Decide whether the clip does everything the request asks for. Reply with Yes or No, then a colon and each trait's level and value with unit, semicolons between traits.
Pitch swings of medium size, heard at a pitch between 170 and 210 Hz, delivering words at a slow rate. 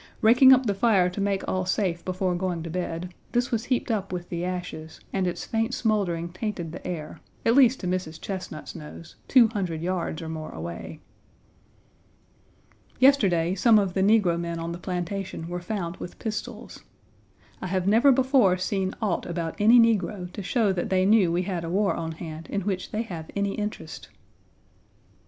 No: average, 3.7 semitones; medium, 185 Hz; average, 185 wpm